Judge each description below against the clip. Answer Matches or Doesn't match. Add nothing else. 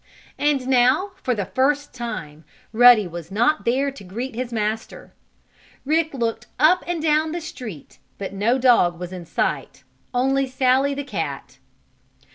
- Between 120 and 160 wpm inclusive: Matches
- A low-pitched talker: Doesn't match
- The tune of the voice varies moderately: Matches